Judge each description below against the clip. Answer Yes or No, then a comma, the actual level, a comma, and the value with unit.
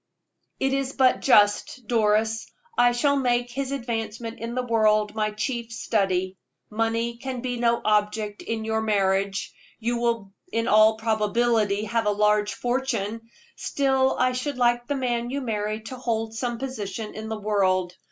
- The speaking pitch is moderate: No, high, 225 Hz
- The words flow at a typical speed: Yes, average, 160 wpm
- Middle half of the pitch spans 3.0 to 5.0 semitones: No, narrow, 2.4 semitones